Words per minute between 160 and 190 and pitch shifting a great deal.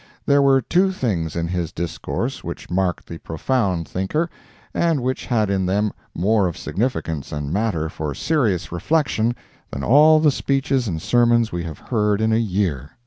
Yes: average, 170 wpm; wide, 7.3 semitones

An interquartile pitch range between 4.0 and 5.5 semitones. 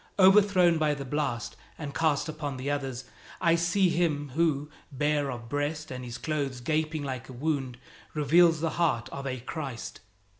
No: average, 3.3 semitones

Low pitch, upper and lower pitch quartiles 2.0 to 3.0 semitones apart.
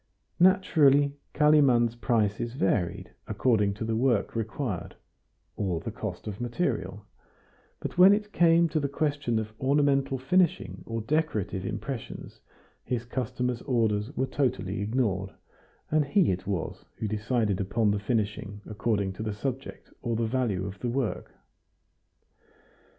No: low, 115 Hz; average, 5.0 semitones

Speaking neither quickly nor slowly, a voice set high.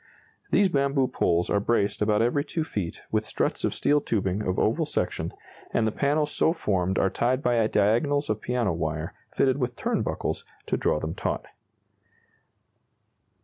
No: average, 165 wpm; low, 115 Hz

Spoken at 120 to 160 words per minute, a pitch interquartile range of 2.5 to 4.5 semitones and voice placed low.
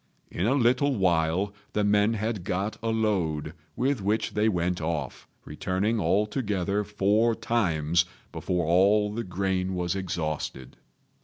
Yes: slow, 135 wpm; average, 3.5 semitones; low, 100 Hz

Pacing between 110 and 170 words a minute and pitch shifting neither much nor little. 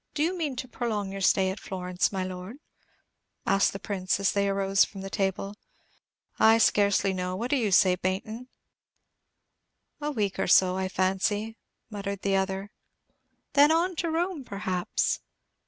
Yes: average, 165 wpm; average, 3.3 semitones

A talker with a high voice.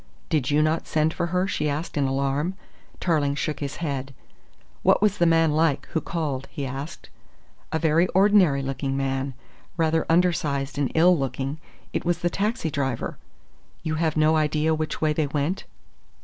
No: medium, 155 Hz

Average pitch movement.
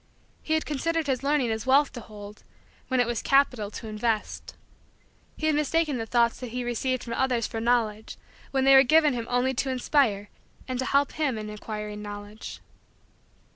Yes: average, 3.8 semitones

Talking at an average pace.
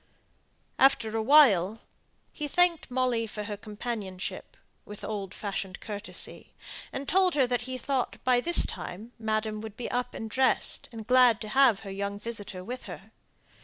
Yes: average, 165 wpm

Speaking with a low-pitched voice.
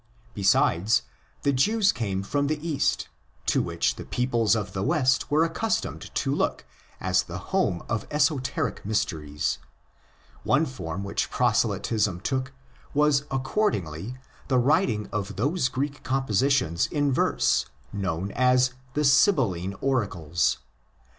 Yes: low, 125 Hz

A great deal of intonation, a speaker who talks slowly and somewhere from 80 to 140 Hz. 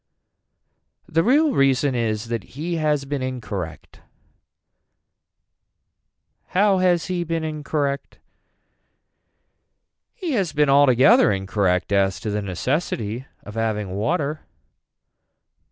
Yes: wide, 7.5 semitones; slow, 100 wpm; low, 135 Hz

